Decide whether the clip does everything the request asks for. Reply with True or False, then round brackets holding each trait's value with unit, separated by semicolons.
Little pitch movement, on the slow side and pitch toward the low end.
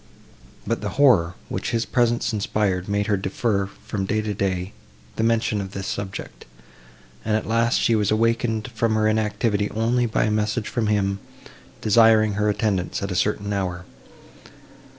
False (2.2 semitones; 165 wpm; 105 Hz)